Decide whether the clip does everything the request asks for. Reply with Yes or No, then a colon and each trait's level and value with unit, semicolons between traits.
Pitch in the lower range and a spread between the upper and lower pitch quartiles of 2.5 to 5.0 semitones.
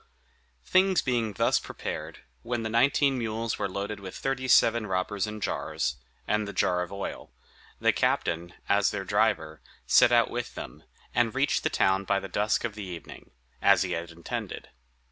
Yes: low, 105 Hz; average, 3.7 semitones